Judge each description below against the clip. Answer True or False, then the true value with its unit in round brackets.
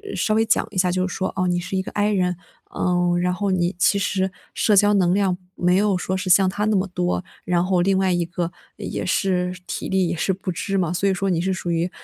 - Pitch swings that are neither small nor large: False (1.7 semitones)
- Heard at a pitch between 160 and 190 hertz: True (185 Hz)